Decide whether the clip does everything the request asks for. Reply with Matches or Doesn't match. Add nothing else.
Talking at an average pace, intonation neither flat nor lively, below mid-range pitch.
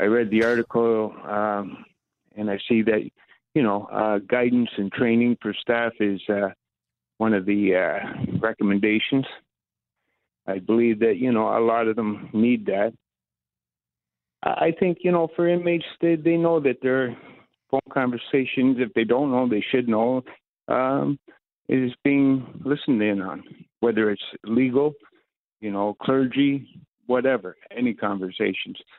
Matches